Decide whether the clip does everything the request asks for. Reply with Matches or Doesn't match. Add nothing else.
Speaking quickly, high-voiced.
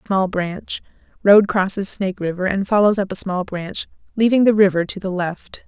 Doesn't match